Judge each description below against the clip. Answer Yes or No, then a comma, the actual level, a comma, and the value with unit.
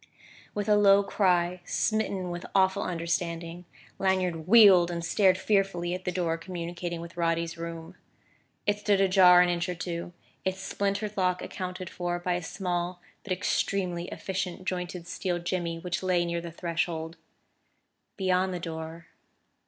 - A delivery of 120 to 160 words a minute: Yes, average, 150 wpm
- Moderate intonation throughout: No, narrow, 1.8 semitones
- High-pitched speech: No, medium, 180 Hz